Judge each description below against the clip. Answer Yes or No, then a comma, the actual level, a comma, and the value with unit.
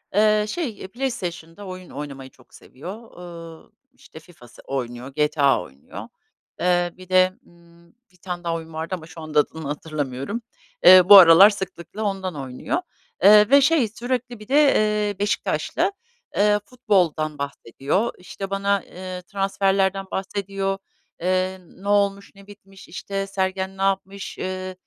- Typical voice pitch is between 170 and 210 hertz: Yes, medium, 185 Hz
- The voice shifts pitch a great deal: No, average, 3.6 semitones